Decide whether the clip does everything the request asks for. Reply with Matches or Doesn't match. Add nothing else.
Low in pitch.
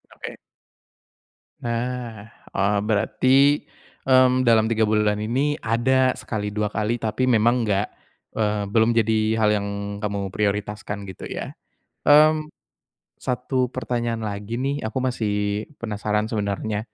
Matches